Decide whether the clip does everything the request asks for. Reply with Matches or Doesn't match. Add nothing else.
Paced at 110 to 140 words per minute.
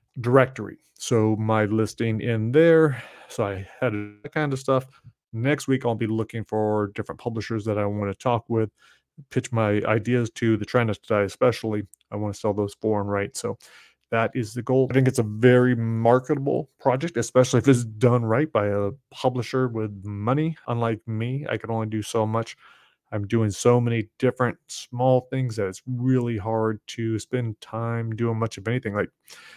Doesn't match